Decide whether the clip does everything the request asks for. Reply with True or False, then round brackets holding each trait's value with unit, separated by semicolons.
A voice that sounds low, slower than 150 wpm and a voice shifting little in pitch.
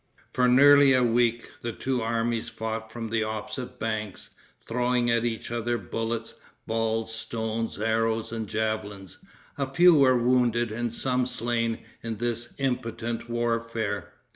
True (115 Hz; 140 wpm; 1.5 semitones)